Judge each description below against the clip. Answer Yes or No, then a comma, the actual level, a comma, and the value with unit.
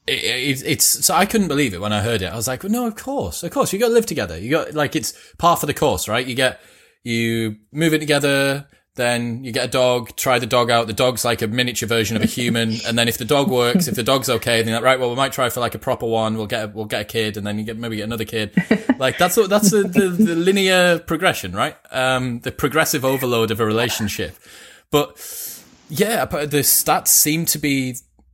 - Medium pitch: No, low, 125 Hz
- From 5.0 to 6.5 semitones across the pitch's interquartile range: Yes, wide, 5.6 semitones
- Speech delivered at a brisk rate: Yes, fast, 255 wpm